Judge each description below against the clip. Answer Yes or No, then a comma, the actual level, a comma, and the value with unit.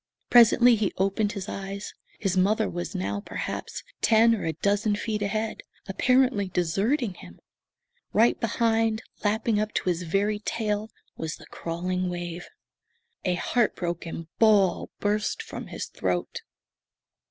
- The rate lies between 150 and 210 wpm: No, slow, 135 wpm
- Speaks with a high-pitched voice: Yes, high, 205 Hz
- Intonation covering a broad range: No, average, 3.3 semitones